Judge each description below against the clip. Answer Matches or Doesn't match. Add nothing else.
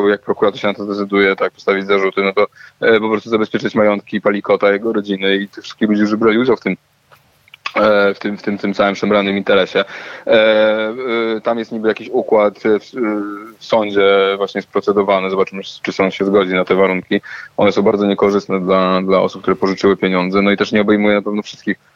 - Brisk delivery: Matches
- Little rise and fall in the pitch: Matches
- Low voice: Matches